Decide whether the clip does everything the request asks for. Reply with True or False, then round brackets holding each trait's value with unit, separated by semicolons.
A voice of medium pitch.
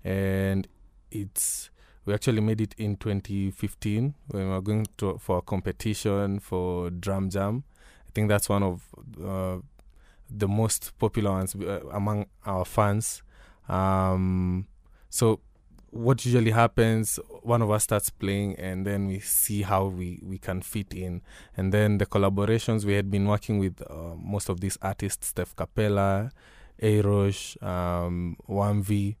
False (100 Hz)